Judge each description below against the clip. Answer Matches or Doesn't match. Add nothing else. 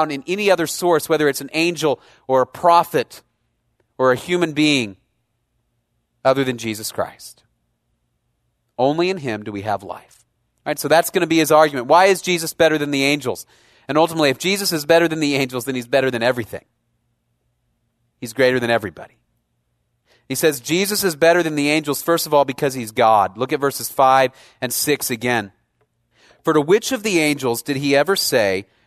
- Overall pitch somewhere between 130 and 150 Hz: Matches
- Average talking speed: Matches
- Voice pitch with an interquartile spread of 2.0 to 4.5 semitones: Doesn't match